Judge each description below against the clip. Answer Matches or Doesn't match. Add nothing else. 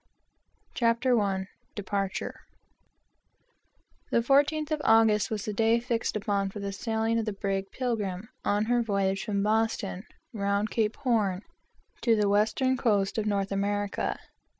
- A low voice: Doesn't match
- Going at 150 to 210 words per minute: Doesn't match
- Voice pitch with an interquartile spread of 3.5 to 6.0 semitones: Doesn't match